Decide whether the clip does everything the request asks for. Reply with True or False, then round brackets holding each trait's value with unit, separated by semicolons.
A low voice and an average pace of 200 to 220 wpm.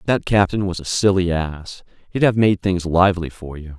True (90 Hz; 205 wpm)